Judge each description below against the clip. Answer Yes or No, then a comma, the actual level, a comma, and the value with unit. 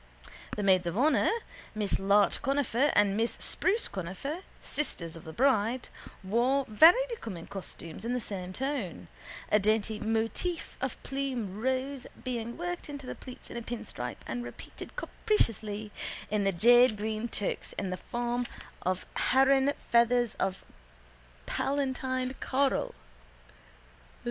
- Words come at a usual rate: No, slow, 130 wpm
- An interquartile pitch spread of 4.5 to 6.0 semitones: Yes, average, 4.8 semitones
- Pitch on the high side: Yes, high, 235 Hz